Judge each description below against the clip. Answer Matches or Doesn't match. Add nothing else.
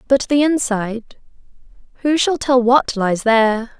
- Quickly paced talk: Doesn't match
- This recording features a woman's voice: Matches